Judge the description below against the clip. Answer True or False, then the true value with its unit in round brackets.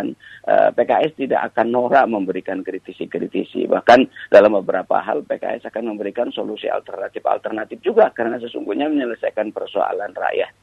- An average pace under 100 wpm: False (125 wpm)